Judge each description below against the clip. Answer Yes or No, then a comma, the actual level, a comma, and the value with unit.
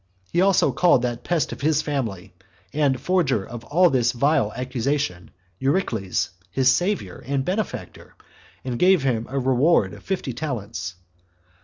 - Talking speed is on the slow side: No, average, 145 wpm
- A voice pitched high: No, low, 135 Hz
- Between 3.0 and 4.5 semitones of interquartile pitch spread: No, average, 5.1 semitones